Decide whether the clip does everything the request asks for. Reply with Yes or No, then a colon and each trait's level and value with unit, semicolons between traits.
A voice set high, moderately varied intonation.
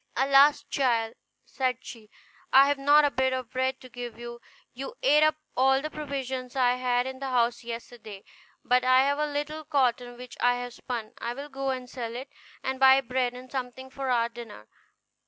No: very high, 255 Hz; narrow, 2.0 semitones